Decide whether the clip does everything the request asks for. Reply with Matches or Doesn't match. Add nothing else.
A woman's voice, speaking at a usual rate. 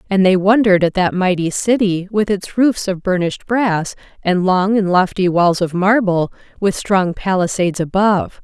Matches